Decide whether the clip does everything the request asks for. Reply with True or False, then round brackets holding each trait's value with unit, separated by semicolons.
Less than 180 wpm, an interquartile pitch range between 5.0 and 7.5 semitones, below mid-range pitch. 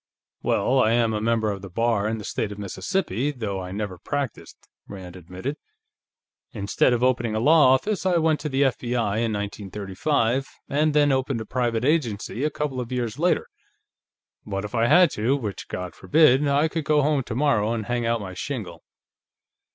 False (185 wpm; 5.3 semitones; 120 Hz)